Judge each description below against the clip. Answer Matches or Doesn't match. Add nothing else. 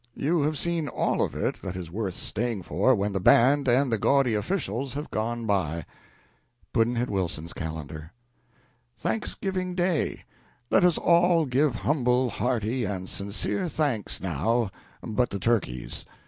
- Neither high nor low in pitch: Doesn't match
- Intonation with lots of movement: Matches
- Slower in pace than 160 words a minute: Matches